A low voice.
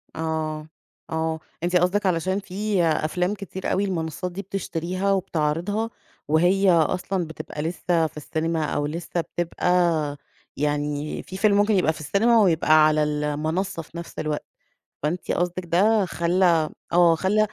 No: medium, 170 Hz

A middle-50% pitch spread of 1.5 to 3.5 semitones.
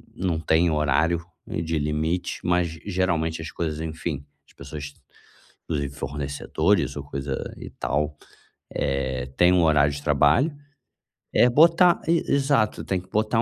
No: average, 3.9 semitones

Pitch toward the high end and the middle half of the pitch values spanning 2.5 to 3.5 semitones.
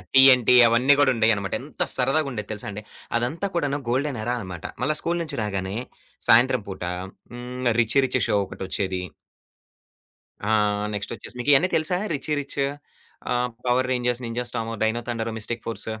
No: low, 120 Hz; average, 3.2 semitones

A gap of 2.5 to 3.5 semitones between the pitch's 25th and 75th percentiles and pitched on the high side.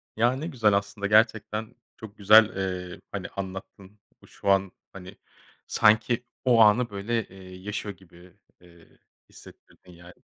No: average, 2.8 semitones; low, 100 Hz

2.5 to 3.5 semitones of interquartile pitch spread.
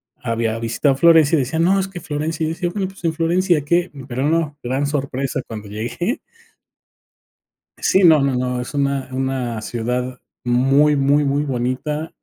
No: average, 4.5 semitones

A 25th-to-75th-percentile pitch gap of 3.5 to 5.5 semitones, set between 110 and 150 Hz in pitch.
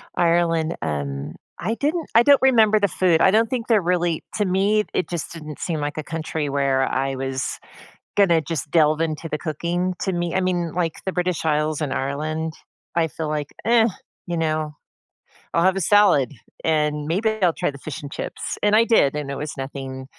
No: average, 3.9 semitones; medium, 165 Hz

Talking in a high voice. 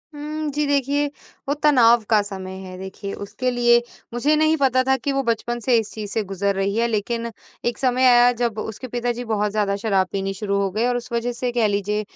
Yes: high, 235 Hz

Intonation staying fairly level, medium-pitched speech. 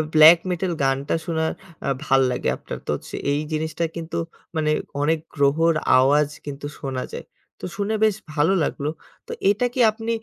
No: average, 3.2 semitones; medium, 155 Hz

